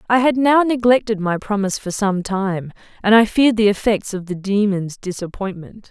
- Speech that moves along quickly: No, average, 185 wpm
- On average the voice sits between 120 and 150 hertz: No, high, 205 Hz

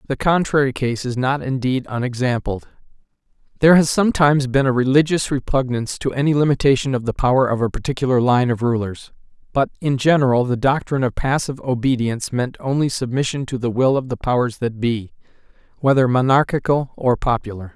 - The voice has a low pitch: Yes, low, 130 Hz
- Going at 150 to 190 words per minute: Yes, average, 165 wpm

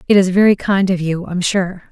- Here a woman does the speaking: Yes, female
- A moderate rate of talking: No, fast, 250 wpm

